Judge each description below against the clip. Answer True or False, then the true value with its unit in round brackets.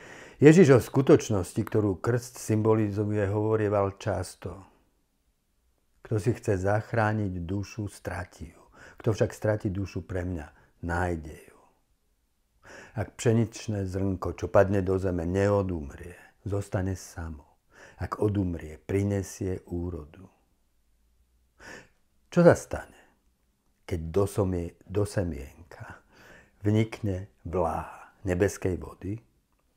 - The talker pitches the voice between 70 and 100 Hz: True (95 Hz)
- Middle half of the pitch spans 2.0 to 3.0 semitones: False (4.9 semitones)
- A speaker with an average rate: False (95 wpm)